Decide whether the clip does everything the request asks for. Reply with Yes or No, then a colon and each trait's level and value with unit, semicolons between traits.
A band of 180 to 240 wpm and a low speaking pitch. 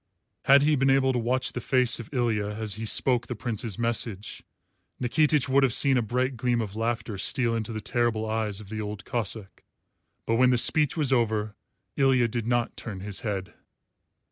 Yes: average, 195 wpm; low, 120 Hz